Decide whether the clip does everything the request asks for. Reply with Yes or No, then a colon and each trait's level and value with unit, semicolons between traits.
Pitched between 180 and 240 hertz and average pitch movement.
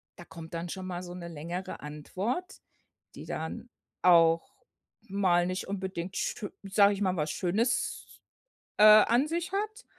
Yes: medium, 185 Hz; average, 3.6 semitones